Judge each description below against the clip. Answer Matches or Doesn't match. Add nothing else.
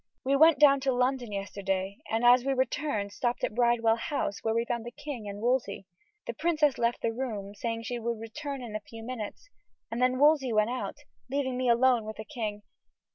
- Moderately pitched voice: Doesn't match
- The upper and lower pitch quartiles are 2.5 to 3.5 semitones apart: Matches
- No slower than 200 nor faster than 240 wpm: Matches